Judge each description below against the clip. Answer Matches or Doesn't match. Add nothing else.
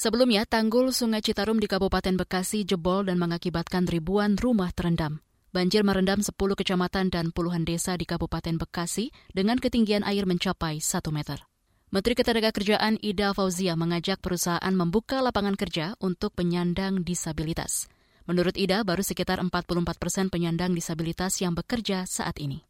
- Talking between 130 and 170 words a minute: Matches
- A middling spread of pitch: Matches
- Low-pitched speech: Doesn't match